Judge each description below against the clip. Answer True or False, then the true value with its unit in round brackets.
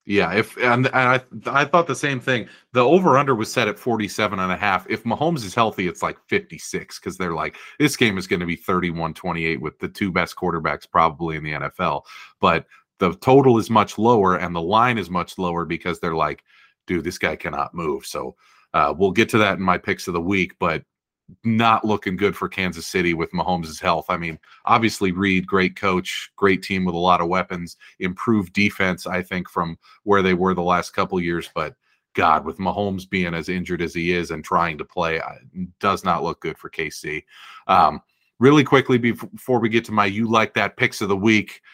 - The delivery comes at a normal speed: False (215 wpm)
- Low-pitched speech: True (95 Hz)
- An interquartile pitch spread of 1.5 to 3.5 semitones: False (4.1 semitones)